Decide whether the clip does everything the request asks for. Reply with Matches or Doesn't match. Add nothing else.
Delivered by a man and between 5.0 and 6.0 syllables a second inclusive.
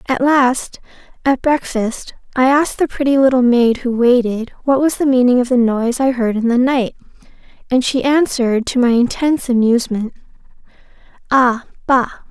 Doesn't match